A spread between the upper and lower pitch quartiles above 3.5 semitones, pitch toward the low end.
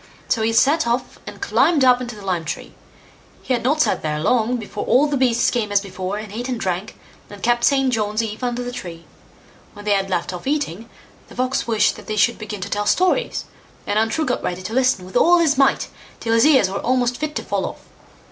No: average, 4.1 semitones; high, 230 Hz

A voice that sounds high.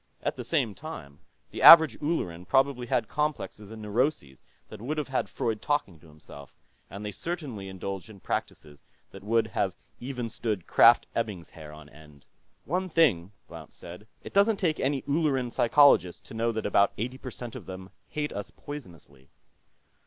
No: low, 115 Hz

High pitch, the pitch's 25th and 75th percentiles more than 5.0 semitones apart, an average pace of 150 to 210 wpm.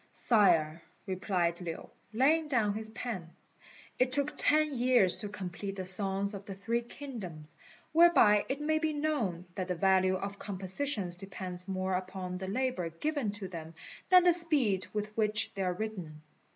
Yes: high, 200 Hz; wide, 5.5 semitones; average, 165 wpm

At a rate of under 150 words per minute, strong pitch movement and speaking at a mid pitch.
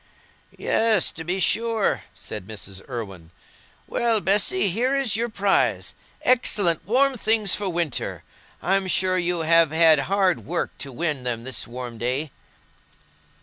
Yes: slow, 135 wpm; wide, 7.5 semitones; medium, 180 Hz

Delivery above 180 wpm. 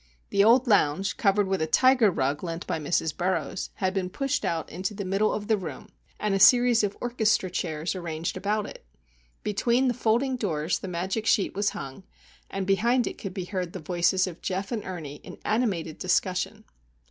Yes: average, 195 wpm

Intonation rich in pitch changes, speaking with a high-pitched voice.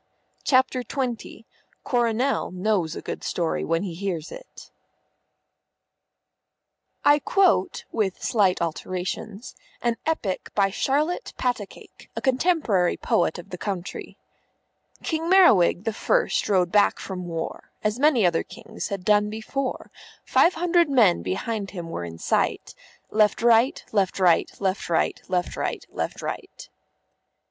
Yes: wide, 6.0 semitones; high, 210 Hz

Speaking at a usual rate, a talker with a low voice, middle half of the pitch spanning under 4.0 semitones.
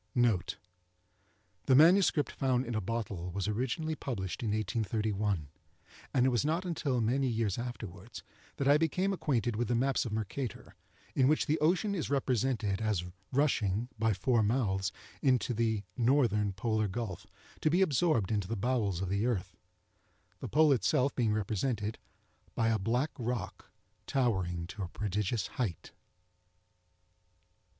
No: average, 145 wpm; low, 115 Hz; average, 4.8 semitones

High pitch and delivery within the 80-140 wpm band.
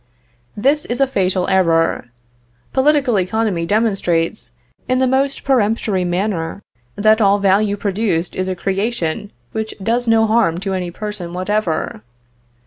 Yes: high, 205 Hz; slow, 135 wpm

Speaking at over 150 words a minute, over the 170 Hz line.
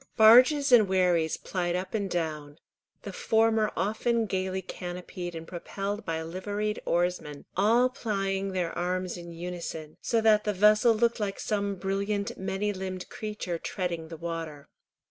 No: average, 145 wpm; high, 190 Hz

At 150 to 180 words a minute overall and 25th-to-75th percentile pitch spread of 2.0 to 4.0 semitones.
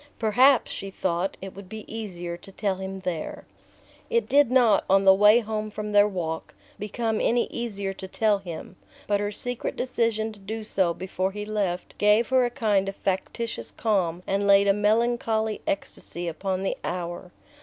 Yes: average, 175 wpm; narrow, 2.5 semitones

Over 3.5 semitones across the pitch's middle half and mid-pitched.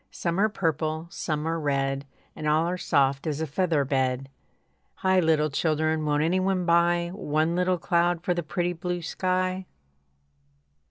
No: average, 2.8 semitones; medium, 165 Hz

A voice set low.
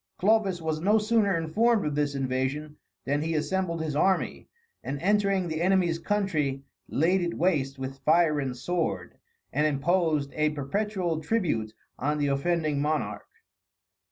No: medium, 160 Hz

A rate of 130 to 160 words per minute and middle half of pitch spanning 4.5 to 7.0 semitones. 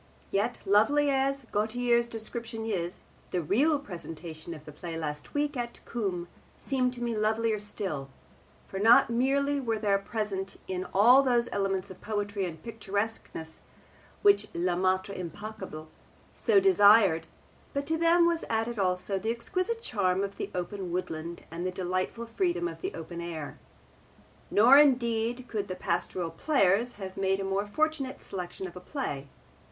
Yes: average, 155 wpm; average, 5.1 semitones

